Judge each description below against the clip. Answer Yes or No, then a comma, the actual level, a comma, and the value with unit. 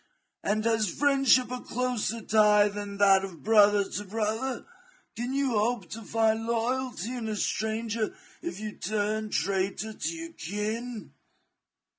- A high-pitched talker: Yes, high, 220 Hz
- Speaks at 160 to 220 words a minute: No, average, 140 wpm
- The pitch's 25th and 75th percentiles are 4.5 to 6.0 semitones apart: No, narrow, 2.4 semitones